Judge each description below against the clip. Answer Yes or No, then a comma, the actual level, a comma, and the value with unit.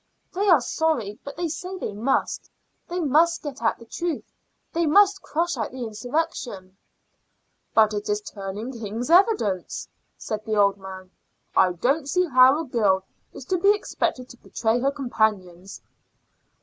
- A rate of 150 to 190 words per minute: Yes, average, 160 wpm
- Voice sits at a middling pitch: No, high, 245 Hz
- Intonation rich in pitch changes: Yes, wide, 7.7 semitones